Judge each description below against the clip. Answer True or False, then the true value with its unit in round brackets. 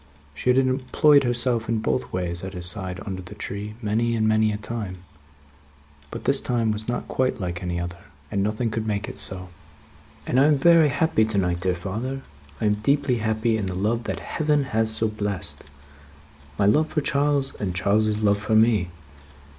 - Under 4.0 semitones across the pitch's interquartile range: False (4.4 semitones)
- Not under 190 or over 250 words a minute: True (195 wpm)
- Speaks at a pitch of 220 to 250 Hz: False (110 Hz)